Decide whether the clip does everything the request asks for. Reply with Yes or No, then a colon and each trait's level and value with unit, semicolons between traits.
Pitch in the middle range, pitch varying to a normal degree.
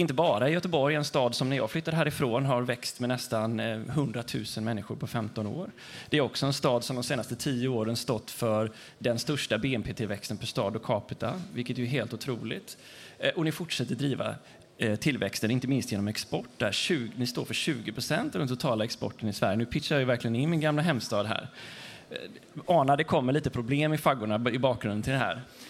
No: low, 125 Hz; average, 4.2 semitones